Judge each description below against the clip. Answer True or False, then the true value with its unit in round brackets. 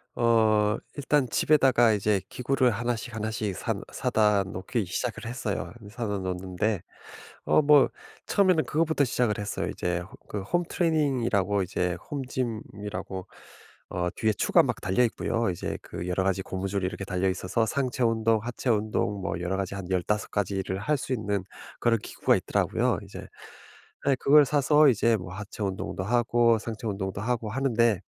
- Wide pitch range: False (4.2 semitones)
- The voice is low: True (110 Hz)